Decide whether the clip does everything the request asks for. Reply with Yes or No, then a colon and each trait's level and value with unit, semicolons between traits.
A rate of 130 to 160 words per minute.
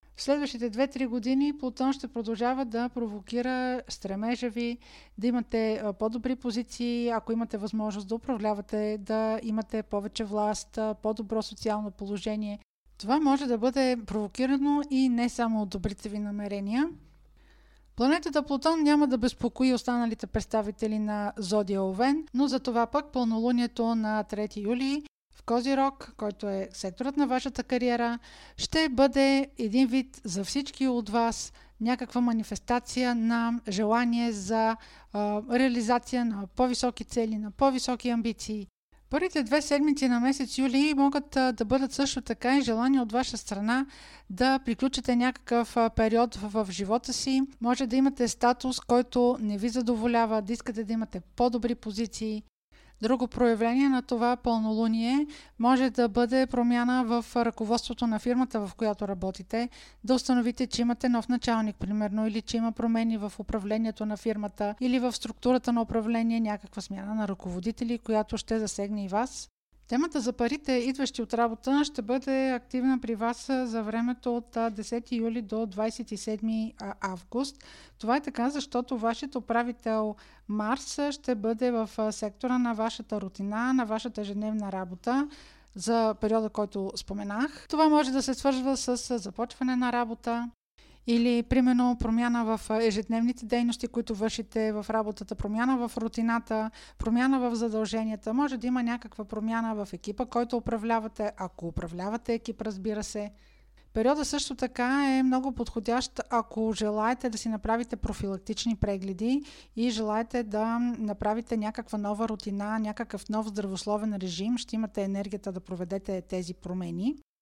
Yes: average, 145 wpm